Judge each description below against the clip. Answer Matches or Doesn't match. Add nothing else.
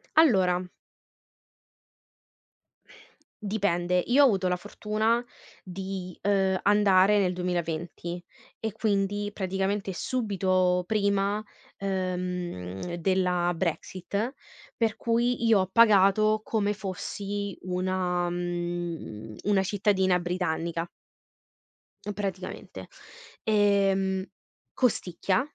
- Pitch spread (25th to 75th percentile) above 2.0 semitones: Matches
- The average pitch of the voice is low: Doesn't match